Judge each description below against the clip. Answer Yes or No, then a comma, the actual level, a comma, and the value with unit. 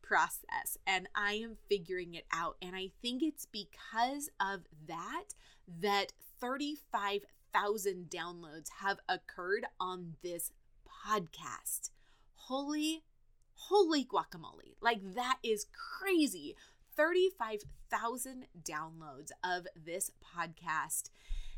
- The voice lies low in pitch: No, high, 205 Hz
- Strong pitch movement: Yes, wide, 8.7 semitones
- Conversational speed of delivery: No, slow, 95 wpm